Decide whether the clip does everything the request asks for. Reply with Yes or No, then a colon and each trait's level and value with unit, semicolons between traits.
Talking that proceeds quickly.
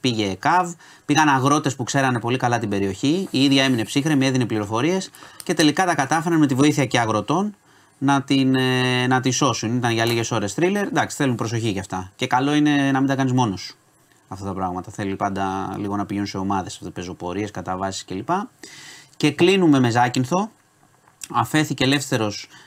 Yes: fast, 180 wpm